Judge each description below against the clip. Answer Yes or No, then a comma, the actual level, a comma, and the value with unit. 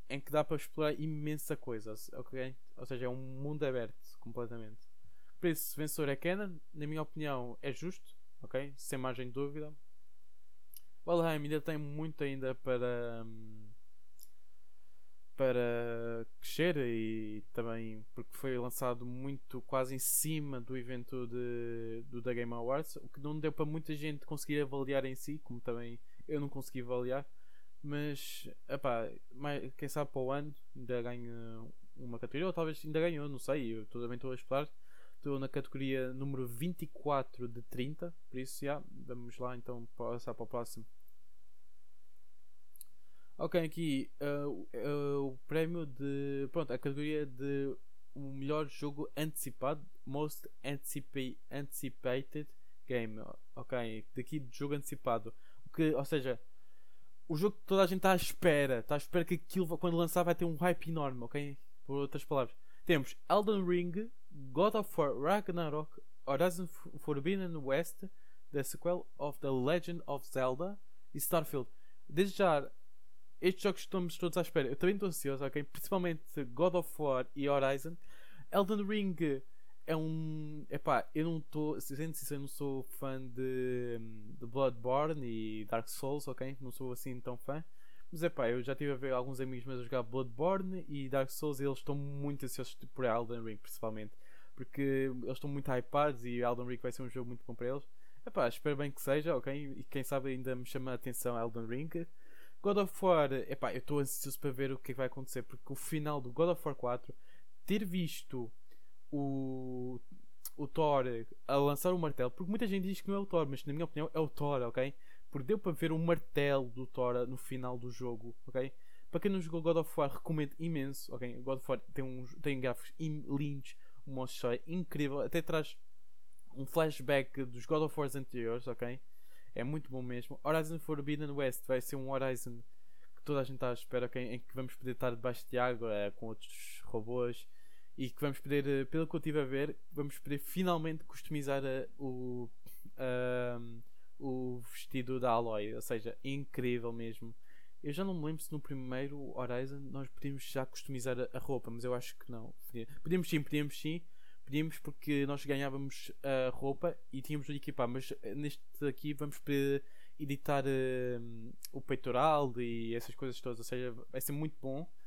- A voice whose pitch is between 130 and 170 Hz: Yes, medium, 140 Hz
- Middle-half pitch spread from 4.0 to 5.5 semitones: No, average, 3.4 semitones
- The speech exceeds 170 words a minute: Yes, average, 180 wpm